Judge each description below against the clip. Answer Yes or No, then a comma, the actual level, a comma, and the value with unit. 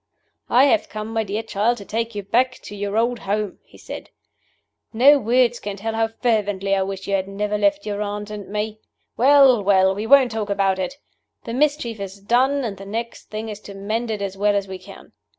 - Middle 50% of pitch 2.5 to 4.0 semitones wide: Yes, average, 2.9 semitones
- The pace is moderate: No, fast, 220 wpm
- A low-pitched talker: No, high, 215 Hz